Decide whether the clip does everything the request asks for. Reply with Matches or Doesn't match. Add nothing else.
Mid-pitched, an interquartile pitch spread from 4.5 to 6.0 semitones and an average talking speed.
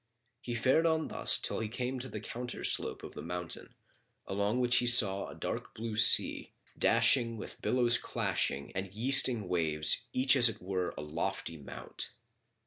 Doesn't match